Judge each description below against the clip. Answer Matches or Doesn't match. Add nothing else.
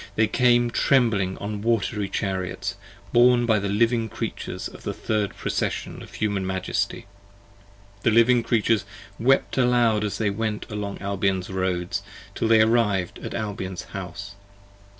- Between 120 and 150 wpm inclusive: Matches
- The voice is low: Matches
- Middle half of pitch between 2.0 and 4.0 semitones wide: Matches